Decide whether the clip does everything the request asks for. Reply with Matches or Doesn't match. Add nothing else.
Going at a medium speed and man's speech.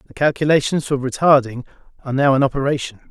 Matches